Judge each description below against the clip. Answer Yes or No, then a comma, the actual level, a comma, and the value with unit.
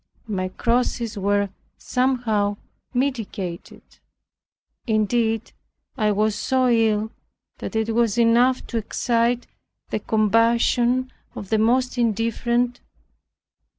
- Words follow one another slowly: Yes, slow, 95 wpm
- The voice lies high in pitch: Yes, high, 230 Hz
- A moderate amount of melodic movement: No, narrow, 2.3 semitones